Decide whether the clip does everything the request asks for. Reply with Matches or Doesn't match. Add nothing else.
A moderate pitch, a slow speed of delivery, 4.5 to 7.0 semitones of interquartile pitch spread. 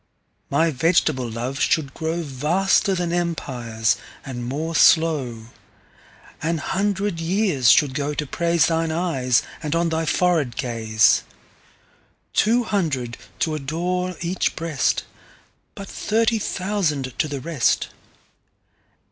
Matches